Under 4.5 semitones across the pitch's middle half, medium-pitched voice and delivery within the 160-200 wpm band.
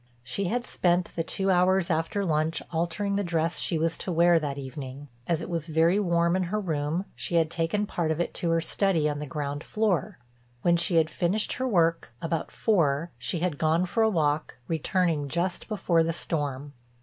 Yes: narrow, 2.6 semitones; medium, 170 Hz; average, 195 wpm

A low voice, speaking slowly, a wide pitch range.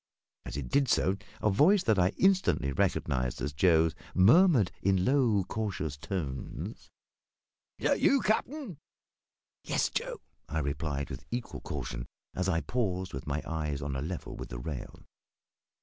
No: very low, 90 Hz; average, 150 wpm; wide, 8.0 semitones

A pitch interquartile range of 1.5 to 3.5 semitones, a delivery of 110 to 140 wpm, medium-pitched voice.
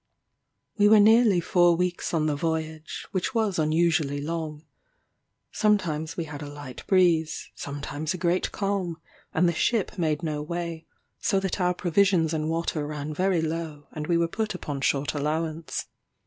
No: average, 2.9 semitones; average, 160 wpm; medium, 165 Hz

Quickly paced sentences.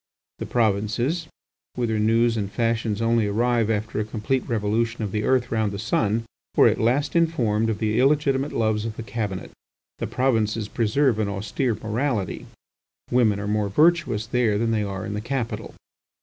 No: average, 170 wpm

